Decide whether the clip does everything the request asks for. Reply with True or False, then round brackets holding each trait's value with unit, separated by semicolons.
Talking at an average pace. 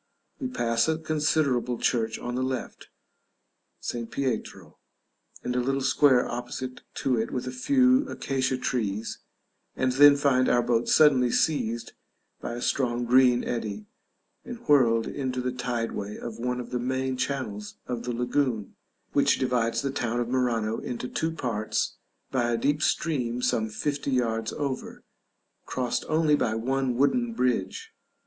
True (155 wpm)